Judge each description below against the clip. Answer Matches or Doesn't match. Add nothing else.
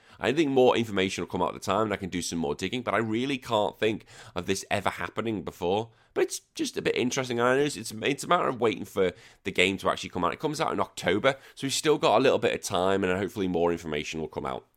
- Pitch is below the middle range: Matches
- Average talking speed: Doesn't match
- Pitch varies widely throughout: Matches